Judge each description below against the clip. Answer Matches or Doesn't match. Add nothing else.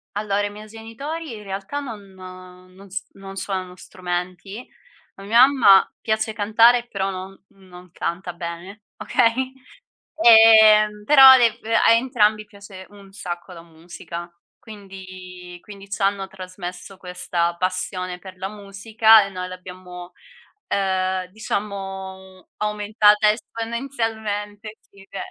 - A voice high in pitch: Matches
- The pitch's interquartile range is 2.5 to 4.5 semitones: Matches